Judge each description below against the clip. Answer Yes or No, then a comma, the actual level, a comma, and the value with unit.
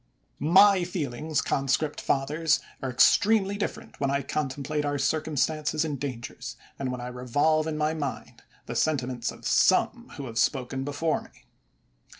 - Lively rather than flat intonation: No, average, 2.9 semitones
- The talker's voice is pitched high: No, medium, 145 Hz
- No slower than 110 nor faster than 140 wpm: No, average, 150 wpm